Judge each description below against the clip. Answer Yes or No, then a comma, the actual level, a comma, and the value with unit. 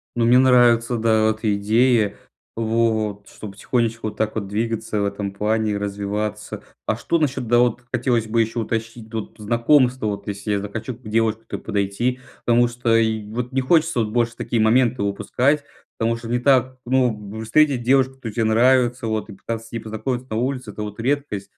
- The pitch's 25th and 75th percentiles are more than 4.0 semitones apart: No, narrow, 2.4 semitones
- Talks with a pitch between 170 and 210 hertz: No, low, 115 Hz